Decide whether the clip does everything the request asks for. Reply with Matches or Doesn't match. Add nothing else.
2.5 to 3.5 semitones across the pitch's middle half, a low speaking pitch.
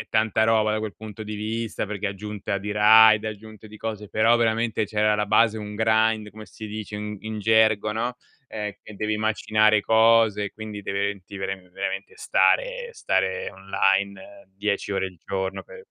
Doesn't match